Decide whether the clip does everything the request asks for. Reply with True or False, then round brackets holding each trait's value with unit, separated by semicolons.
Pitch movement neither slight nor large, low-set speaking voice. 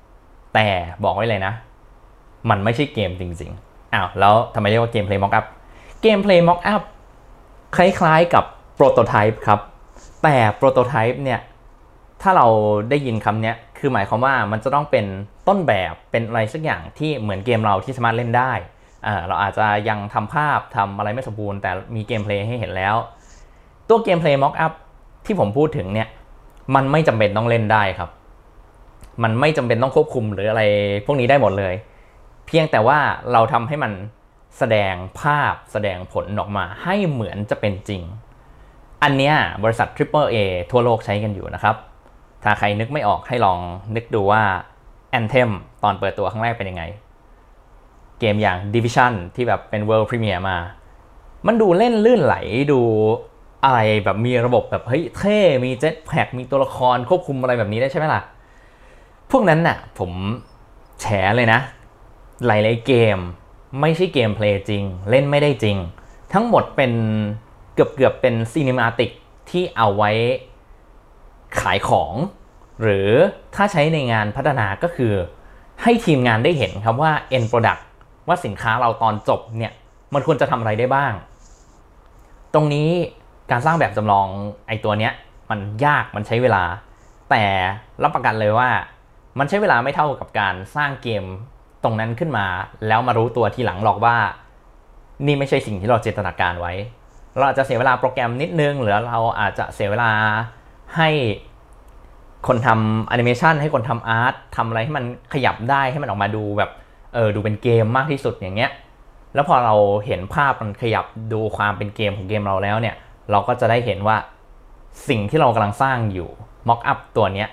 True (4.2 semitones; 115 Hz)